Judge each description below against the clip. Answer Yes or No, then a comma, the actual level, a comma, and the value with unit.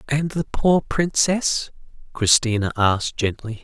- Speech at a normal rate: No, slow, 115 wpm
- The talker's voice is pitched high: No, low, 135 Hz